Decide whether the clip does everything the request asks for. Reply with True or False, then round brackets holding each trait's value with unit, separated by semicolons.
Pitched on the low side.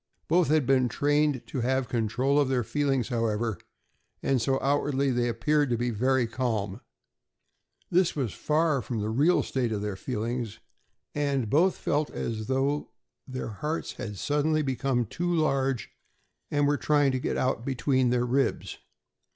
True (130 Hz)